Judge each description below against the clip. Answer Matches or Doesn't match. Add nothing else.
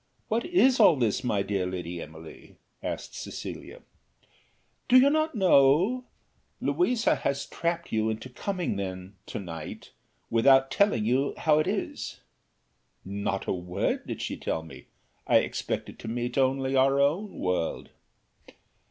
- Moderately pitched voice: Doesn't match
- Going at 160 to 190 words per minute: Doesn't match